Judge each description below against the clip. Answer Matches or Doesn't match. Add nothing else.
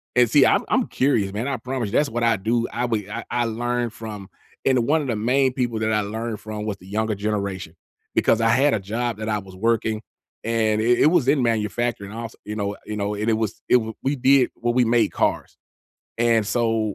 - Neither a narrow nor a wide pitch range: Doesn't match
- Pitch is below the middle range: Matches